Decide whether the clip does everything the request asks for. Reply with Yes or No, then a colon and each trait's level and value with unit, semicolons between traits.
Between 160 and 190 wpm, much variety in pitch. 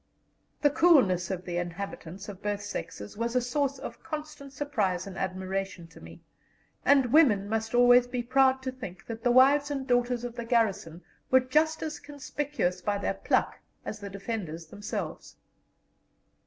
Yes: average, 165 wpm; wide, 5.7 semitones